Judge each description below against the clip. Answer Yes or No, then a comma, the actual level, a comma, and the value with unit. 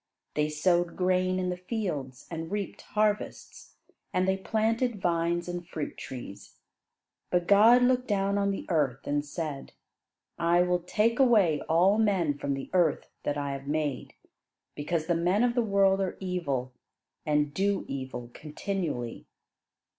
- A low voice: No, medium, 175 Hz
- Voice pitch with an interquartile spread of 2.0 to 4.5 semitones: No, average, 5.0 semitones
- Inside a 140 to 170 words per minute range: Yes, average, 150 wpm